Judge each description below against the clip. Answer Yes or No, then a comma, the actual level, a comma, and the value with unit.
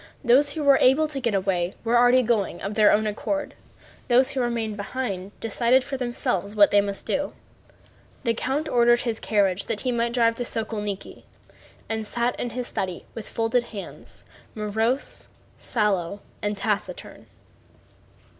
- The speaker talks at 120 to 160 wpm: Yes, average, 155 wpm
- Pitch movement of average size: Yes, average, 3.3 semitones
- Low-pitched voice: No, high, 230 Hz